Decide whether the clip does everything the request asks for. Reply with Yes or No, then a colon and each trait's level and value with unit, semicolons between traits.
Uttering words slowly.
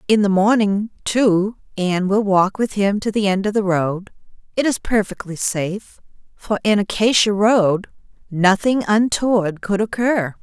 No: average, 155 wpm